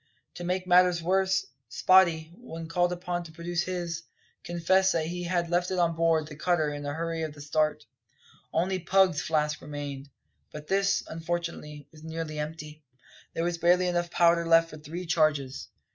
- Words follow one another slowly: No, average, 175 wpm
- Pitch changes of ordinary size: No, narrow, 2.3 semitones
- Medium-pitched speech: Yes, medium, 170 Hz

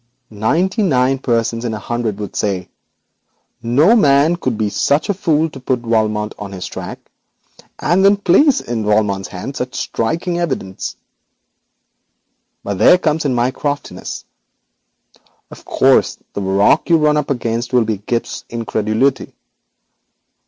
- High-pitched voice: No, low, 120 Hz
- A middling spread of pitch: No, wide, 5.9 semitones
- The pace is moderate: Yes, average, 145 wpm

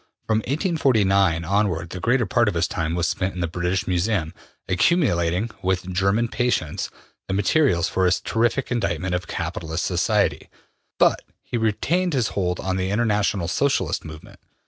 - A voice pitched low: Yes, very low, 95 Hz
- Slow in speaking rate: No, average, 155 wpm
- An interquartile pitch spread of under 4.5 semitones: No, average, 4.9 semitones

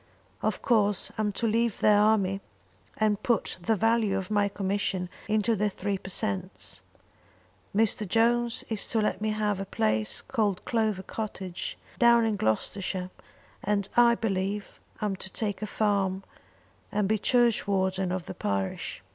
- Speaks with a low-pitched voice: No, high, 205 Hz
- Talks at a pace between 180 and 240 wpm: No, average, 150 wpm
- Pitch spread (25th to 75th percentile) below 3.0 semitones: Yes, narrow, 2.4 semitones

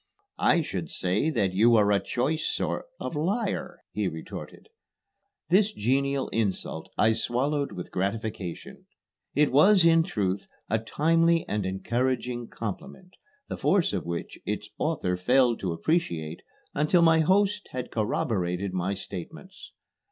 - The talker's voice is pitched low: Yes, low, 120 Hz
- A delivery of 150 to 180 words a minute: No, slow, 135 wpm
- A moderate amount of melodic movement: No, wide, 8.7 semitones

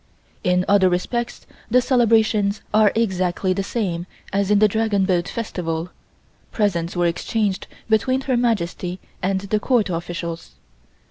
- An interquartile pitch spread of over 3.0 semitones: Yes, average, 3.7 semitones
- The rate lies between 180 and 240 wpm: No, slow, 135 wpm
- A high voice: Yes, high, 200 Hz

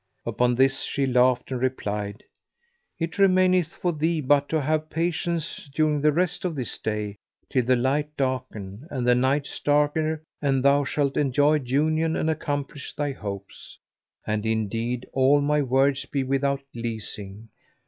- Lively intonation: No, average, 3.5 semitones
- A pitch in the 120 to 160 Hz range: Yes, medium, 140 Hz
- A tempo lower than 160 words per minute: Yes, average, 150 wpm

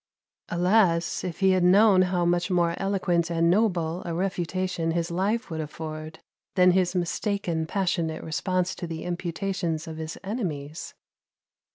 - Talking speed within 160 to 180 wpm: No, average, 145 wpm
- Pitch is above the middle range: No, medium, 175 Hz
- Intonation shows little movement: Yes, narrow, 2.3 semitones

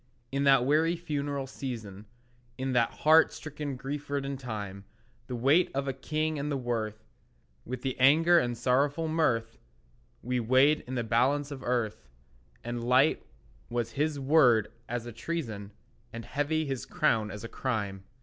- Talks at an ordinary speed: Yes, average, 155 wpm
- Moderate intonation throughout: Yes, average, 3.8 semitones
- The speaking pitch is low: Yes, low, 130 Hz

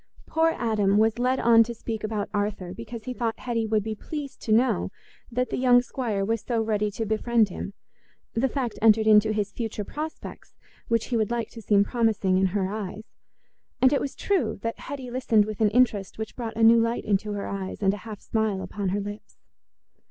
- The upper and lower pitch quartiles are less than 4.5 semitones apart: Yes, narrow, 2.4 semitones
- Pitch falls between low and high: No, high, 220 Hz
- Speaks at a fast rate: Yes, fast, 210 wpm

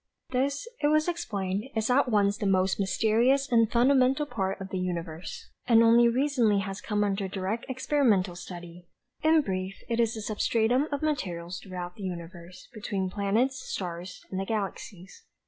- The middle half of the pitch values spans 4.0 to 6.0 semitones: Yes, average, 5.1 semitones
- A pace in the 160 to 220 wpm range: Yes, average, 165 wpm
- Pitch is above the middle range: Yes, high, 210 Hz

